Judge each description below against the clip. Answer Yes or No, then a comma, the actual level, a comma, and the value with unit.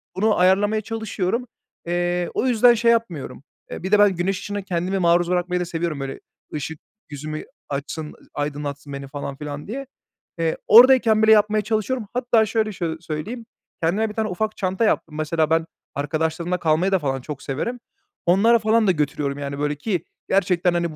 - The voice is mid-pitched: Yes, medium, 180 Hz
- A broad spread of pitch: Yes, wide, 5.8 semitones